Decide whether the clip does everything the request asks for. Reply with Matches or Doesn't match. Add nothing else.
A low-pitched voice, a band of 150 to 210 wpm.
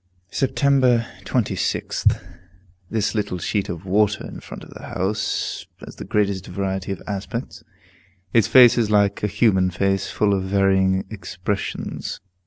Doesn't match